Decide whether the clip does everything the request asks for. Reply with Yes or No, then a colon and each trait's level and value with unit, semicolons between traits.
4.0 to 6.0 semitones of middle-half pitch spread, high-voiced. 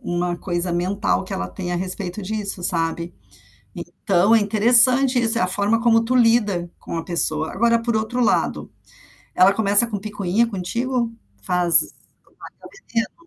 Yes: average, 4.6 semitones; high, 200 Hz